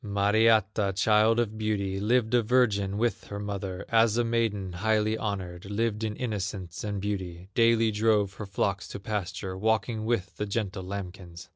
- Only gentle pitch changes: Yes, narrow, 2.3 semitones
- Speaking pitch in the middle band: No, low, 105 Hz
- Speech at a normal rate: Yes, average, 160 wpm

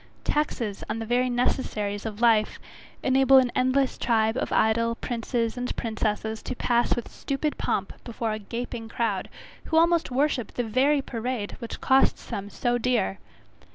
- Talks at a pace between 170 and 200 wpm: No, average, 155 wpm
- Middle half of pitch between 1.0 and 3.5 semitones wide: Yes, average, 2.7 semitones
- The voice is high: Yes, high, 240 Hz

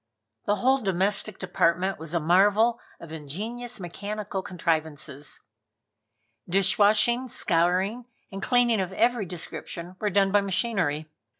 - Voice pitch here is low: No, high, 195 Hz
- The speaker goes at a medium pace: No, slow, 115 wpm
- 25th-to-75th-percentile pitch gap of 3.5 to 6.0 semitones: Yes, average, 3.9 semitones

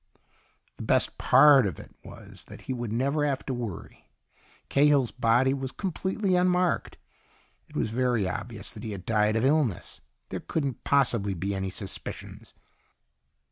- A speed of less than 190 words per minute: Yes, average, 150 wpm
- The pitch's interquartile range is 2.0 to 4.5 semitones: No, average, 5.1 semitones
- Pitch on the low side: Yes, low, 125 Hz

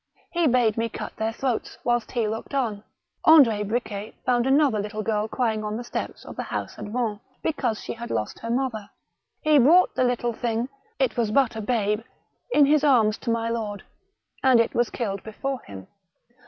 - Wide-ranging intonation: No, average, 3.2 semitones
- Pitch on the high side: Yes, high, 230 Hz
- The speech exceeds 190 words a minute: Yes, average, 200 wpm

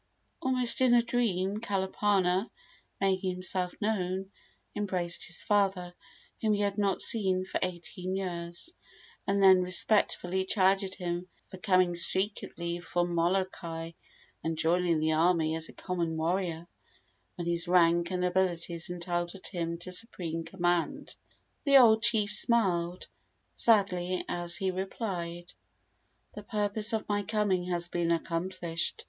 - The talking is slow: Yes, slow, 130 wpm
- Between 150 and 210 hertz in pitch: Yes, medium, 185 Hz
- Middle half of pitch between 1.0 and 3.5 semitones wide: Yes, narrow, 2.5 semitones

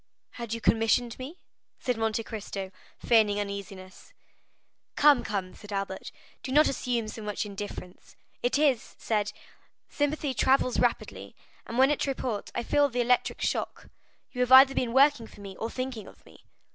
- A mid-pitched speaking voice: No, high, 230 Hz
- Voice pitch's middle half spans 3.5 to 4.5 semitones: Yes, average, 4.0 semitones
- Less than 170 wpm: Yes, average, 160 wpm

